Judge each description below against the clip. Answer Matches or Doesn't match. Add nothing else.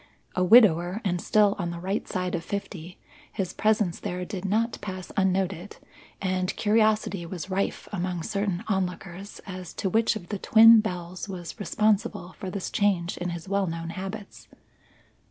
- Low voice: Doesn't match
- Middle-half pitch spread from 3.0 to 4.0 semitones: Doesn't match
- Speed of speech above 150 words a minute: Matches